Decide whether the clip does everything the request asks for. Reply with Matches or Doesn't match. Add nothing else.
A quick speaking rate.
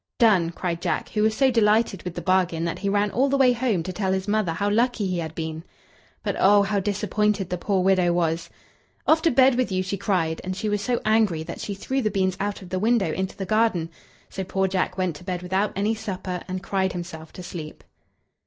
Matches